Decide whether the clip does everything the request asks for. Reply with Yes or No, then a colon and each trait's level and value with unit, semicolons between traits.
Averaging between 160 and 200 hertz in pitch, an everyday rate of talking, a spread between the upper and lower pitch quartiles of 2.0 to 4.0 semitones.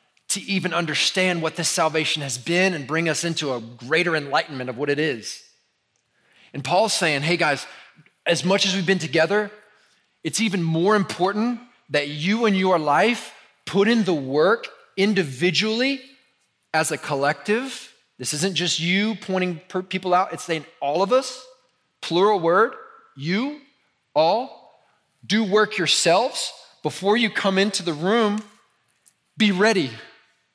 No: medium, 185 Hz; average, 145 wpm; average, 5.0 semitones